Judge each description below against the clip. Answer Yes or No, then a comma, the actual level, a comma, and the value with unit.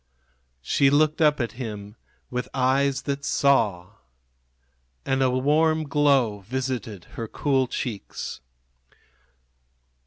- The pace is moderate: No, slow, 100 wpm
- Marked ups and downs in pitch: No, average, 3.7 semitones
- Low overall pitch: Yes, low, 130 Hz